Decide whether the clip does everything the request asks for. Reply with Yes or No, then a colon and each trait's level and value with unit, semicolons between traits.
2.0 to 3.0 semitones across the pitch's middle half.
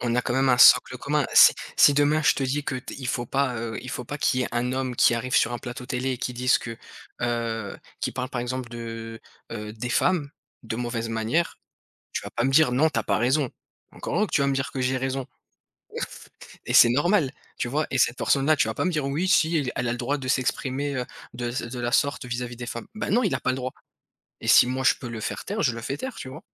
Yes: average, 2.7 semitones